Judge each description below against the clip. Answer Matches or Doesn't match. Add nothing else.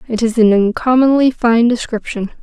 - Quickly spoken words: Doesn't match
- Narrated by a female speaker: Matches